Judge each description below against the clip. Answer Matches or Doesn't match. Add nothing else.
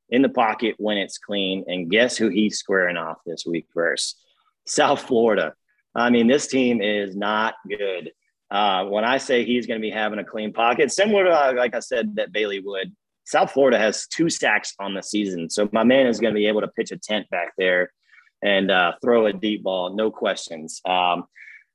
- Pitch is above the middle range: Doesn't match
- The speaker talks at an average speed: Doesn't match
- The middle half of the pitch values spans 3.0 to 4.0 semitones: Matches